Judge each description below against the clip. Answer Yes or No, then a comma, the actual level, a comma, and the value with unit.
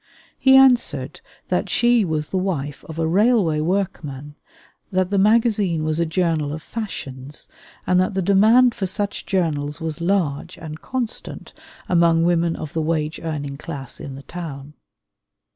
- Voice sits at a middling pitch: Yes, medium, 170 Hz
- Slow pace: No, average, 155 wpm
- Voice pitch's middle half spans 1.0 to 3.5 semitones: No, average, 4.5 semitones